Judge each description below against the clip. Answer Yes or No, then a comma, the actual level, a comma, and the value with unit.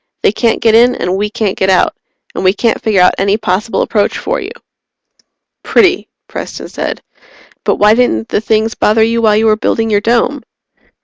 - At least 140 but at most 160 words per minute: No, average, 190 wpm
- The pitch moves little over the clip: Yes, narrow, 2.2 semitones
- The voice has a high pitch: Yes, high, 220 Hz